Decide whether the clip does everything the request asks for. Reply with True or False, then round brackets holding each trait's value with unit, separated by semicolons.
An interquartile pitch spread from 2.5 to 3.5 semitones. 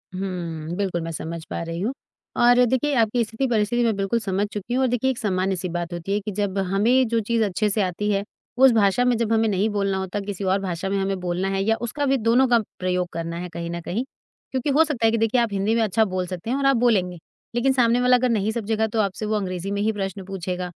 False (3.9 semitones)